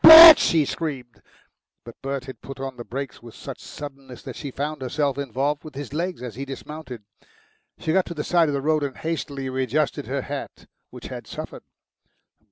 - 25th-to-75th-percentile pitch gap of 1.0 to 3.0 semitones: Yes, average, 2.7 semitones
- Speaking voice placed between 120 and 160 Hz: Yes, medium, 140 Hz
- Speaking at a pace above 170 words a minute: Yes, average, 190 wpm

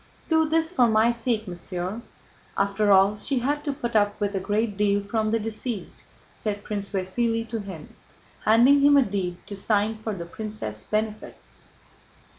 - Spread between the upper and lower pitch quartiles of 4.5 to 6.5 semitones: No, average, 2.8 semitones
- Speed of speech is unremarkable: Yes, average, 175 wpm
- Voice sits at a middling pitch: No, high, 215 Hz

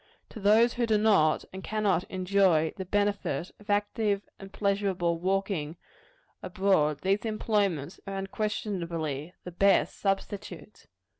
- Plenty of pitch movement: No, average, 2.8 semitones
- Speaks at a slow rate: Yes, slow, 125 wpm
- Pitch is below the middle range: No, high, 195 Hz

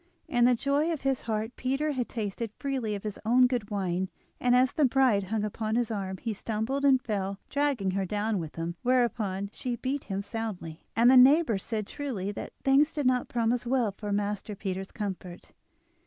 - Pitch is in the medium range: No, high, 225 Hz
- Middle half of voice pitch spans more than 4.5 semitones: No, average, 4.2 semitones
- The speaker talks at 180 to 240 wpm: Yes, average, 195 wpm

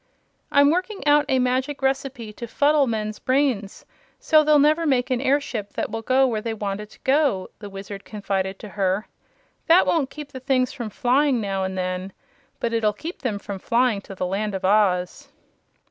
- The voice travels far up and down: Yes, wide, 5.7 semitones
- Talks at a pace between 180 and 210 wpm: Yes, average, 190 wpm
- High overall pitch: Yes, high, 235 Hz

